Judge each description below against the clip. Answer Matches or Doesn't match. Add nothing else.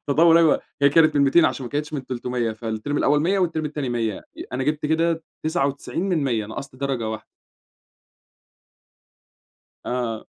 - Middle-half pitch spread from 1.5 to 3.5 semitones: Doesn't match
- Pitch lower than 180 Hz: Matches